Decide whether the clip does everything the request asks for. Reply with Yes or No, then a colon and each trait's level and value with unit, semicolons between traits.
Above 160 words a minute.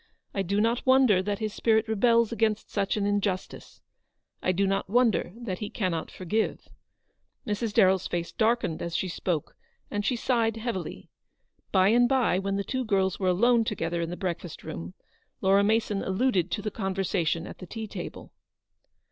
Yes: average, 175 wpm